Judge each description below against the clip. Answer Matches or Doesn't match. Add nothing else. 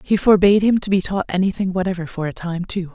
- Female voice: Matches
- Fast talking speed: Matches